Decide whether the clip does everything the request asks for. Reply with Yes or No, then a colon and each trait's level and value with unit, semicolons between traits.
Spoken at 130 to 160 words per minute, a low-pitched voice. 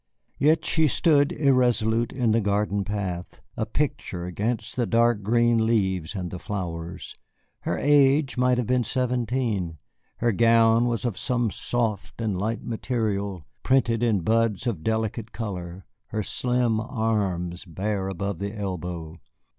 Yes: average, 140 wpm; low, 110 Hz